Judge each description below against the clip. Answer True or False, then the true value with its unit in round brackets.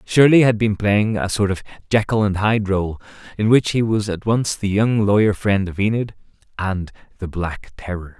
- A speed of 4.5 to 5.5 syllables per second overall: True (4.9 syllables/s)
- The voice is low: True (105 Hz)